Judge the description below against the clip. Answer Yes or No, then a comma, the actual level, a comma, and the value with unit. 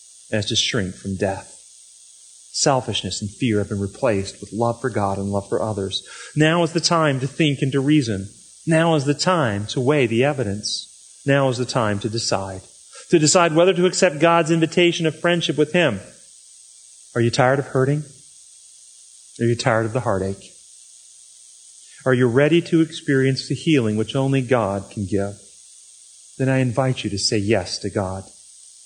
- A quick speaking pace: No, average, 175 wpm